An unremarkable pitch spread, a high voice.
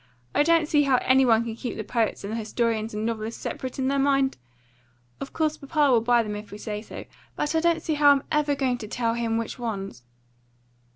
Yes: average, 4.2 semitones; high, 245 Hz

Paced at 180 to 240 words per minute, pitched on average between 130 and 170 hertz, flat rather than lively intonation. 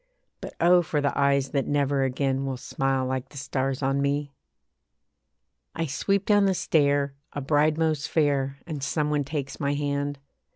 No: average, 170 wpm; medium, 140 Hz; narrow, 1.8 semitones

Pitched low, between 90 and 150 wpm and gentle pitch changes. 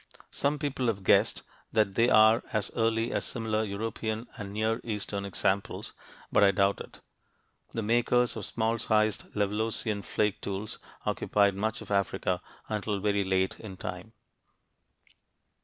Yes: low, 110 Hz; average, 140 wpm; narrow, 2.0 semitones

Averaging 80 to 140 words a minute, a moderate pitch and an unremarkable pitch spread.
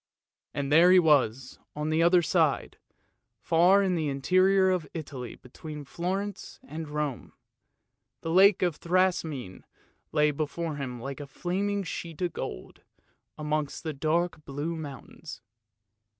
Yes: slow, 135 wpm; medium, 160 Hz; average, 3.7 semitones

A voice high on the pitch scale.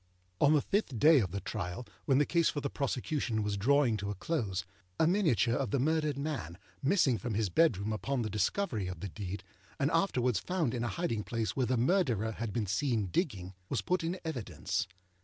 No: low, 125 Hz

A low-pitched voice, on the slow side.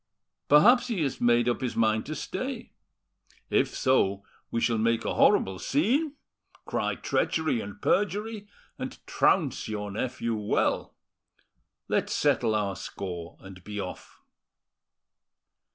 Yes: low, 115 Hz; slow, 125 wpm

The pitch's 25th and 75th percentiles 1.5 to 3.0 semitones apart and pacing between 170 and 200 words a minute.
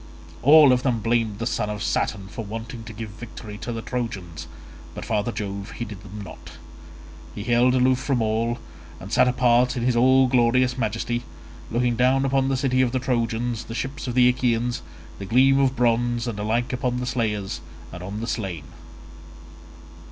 Yes: narrow, 2.5 semitones; average, 180 wpm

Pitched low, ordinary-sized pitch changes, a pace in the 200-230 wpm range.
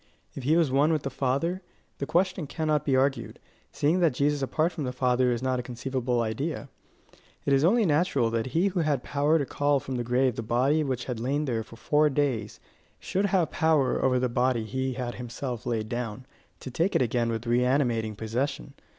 Yes: low, 130 Hz; average, 3.6 semitones; fast, 205 wpm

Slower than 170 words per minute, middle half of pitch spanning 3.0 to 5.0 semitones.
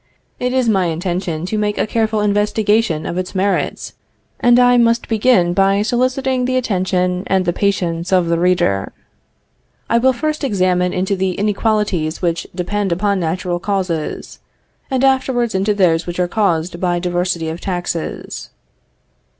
Yes: average, 150 wpm; average, 3.9 semitones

